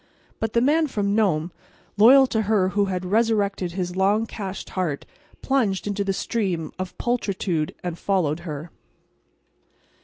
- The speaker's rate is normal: Yes, average, 145 wpm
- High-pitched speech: Yes, high, 195 Hz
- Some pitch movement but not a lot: Yes, average, 3.5 semitones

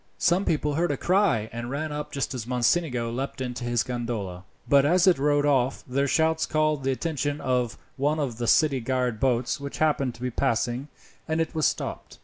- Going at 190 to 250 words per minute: Yes, average, 200 wpm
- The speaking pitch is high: No, low, 135 Hz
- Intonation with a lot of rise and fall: No, average, 3.9 semitones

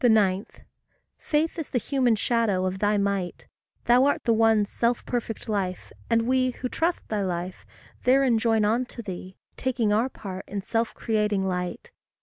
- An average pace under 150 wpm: No, average, 165 wpm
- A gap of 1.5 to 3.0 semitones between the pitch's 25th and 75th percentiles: No, average, 3.7 semitones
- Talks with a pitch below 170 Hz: No, high, 220 Hz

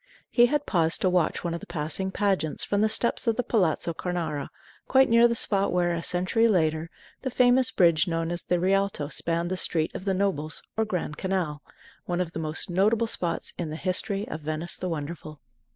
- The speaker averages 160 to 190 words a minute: No, fast, 205 wpm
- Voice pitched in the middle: Yes, medium, 180 Hz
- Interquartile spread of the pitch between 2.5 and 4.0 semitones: Yes, average, 3.7 semitones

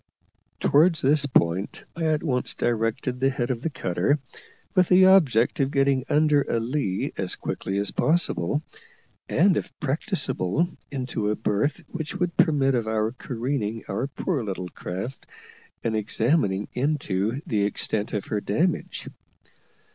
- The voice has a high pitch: No, low, 130 Hz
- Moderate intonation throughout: No, wide, 5.9 semitones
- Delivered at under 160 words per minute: Yes, average, 145 wpm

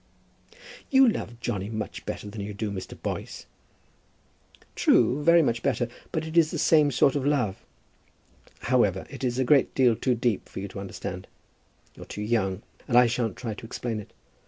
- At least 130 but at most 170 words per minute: No, average, 180 wpm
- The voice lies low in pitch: Yes, low, 120 Hz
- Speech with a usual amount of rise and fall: Yes, average, 4.8 semitones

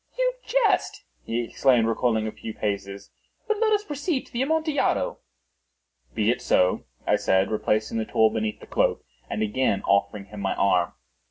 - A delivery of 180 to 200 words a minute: No, average, 170 wpm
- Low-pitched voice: Yes, low, 110 Hz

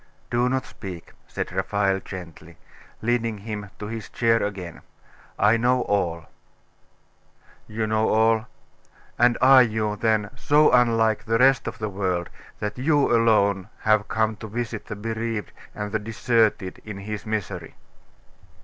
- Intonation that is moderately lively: No, narrow, 2.2 semitones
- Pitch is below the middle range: Yes, low, 110 Hz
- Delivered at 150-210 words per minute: No, average, 140 wpm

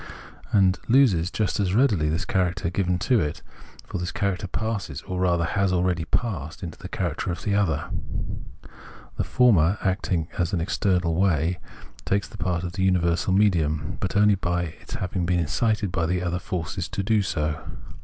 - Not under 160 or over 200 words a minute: Yes, average, 175 wpm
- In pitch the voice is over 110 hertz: No, very low, 90 Hz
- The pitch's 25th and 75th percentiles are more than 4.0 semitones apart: No, average, 2.7 semitones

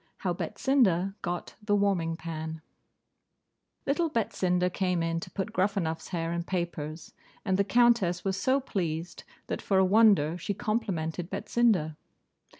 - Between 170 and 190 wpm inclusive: No, average, 140 wpm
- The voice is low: No, medium, 185 Hz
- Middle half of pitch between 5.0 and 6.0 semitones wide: No, average, 3.7 semitones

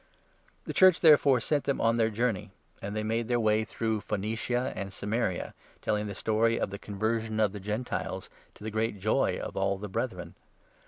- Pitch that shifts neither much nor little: No, narrow, 2.1 semitones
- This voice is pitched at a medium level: No, low, 110 Hz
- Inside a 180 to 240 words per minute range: Yes, average, 195 wpm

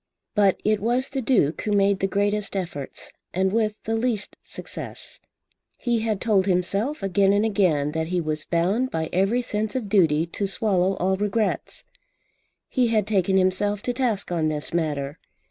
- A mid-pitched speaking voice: No, high, 200 Hz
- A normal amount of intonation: Yes, average, 3.5 semitones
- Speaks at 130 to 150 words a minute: No, average, 170 wpm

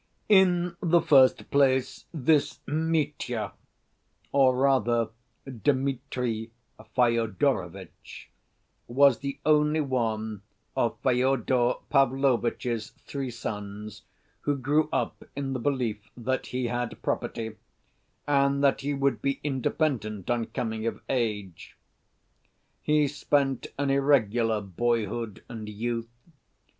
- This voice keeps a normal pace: No, slow, 105 wpm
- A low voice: Yes, low, 130 Hz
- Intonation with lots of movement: No, average, 3.5 semitones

